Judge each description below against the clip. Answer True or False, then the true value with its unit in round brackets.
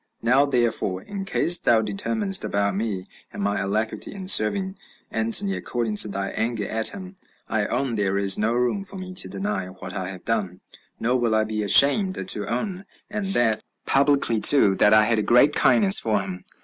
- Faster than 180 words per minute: True (190 wpm)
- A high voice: False (115 Hz)